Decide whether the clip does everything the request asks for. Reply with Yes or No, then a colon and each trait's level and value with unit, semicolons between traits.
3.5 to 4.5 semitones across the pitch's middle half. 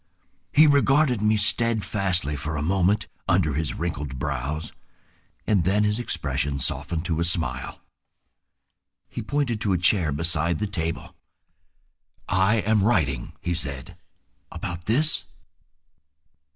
No: wide, 5.5 semitones